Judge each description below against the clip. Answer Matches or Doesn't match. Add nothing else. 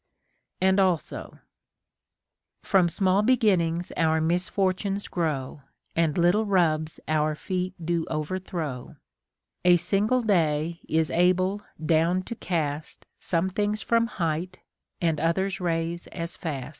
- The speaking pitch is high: Doesn't match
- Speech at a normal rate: Doesn't match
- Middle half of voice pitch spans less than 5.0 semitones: Matches